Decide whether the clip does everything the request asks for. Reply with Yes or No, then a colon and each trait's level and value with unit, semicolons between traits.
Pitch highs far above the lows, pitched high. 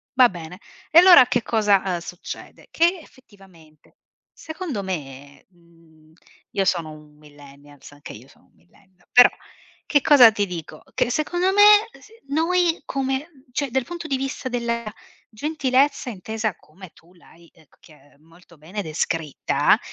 Yes: wide, 8.7 semitones; high, 195 Hz